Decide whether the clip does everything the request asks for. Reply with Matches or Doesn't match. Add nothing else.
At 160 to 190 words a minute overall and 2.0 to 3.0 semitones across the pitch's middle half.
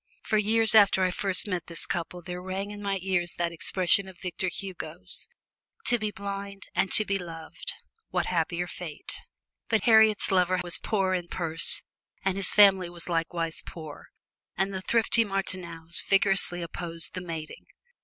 Matches